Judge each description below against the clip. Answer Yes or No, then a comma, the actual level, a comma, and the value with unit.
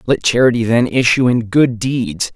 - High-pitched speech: No, low, 120 Hz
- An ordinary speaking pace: Yes, average, 180 wpm